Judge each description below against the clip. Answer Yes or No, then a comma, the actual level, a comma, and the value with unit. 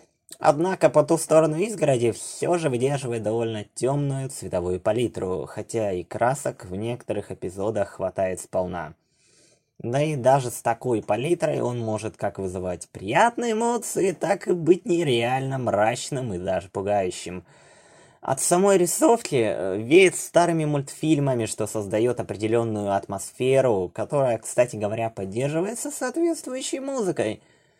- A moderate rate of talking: Yes, average, 125 wpm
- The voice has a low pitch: Yes, low, 130 Hz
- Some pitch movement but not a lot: No, wide, 7.6 semitones